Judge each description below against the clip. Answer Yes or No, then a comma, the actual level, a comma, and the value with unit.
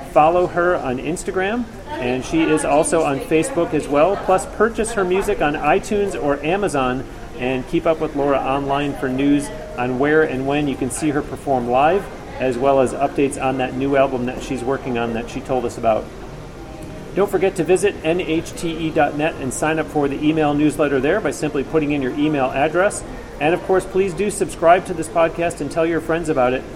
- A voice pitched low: No, medium, 150 Hz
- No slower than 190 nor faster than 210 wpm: Yes, average, 200 wpm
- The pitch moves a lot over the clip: No, average, 4.0 semitones